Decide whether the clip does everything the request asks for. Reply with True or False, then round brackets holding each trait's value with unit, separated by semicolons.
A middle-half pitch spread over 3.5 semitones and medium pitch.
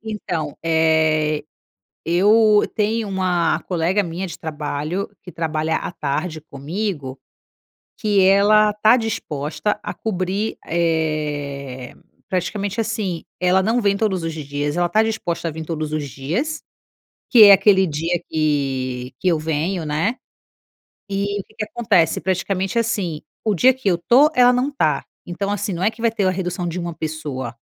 True (4.9 semitones; 175 Hz)